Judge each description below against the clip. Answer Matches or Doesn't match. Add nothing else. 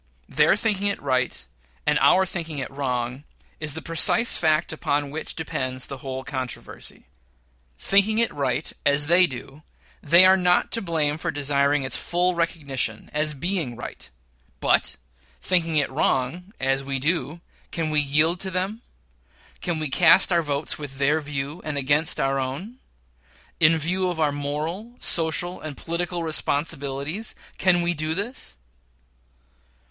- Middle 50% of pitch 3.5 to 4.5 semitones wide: Matches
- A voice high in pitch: Doesn't match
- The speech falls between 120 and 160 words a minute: Matches